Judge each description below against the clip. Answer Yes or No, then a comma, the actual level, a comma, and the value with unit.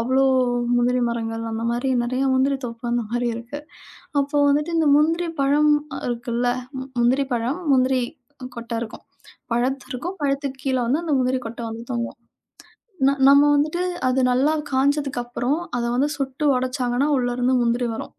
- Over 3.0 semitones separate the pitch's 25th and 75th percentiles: No, average, 2.7 semitones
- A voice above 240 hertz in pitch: Yes, very high, 255 Hz